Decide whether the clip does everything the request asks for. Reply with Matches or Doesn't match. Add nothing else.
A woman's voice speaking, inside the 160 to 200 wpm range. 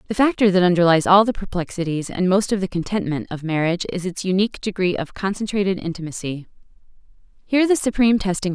Matches